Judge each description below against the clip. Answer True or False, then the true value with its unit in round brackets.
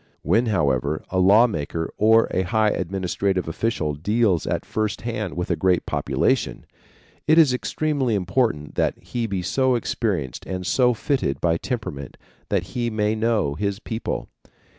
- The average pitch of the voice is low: True (105 Hz)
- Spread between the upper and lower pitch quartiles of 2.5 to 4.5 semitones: False (4.9 semitones)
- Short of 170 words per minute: True (155 wpm)